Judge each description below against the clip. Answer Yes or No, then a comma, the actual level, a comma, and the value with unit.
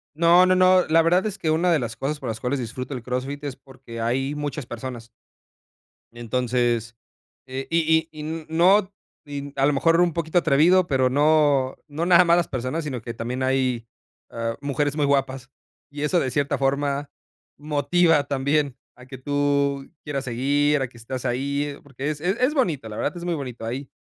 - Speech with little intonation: No, average, 3.6 semitones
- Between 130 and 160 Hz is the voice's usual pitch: Yes, medium, 140 Hz